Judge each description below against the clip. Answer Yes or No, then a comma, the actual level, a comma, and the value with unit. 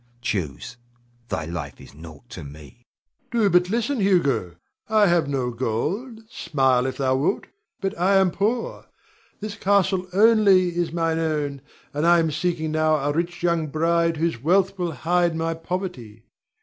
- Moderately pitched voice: Yes, medium, 165 Hz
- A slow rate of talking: No, average, 160 wpm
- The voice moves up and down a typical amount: No, wide, 5.8 semitones